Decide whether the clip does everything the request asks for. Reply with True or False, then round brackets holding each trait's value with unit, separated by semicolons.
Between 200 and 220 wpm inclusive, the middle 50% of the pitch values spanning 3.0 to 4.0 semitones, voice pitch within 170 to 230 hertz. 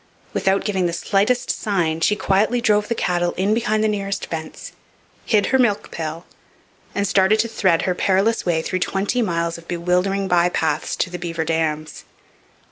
False (170 wpm; 3.6 semitones; 190 Hz)